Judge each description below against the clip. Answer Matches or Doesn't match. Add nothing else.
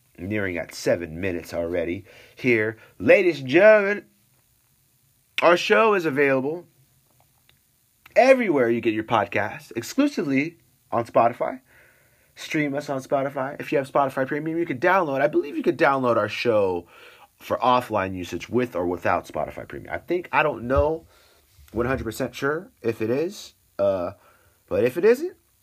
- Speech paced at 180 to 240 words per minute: Doesn't match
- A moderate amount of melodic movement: Doesn't match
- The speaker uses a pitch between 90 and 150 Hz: Matches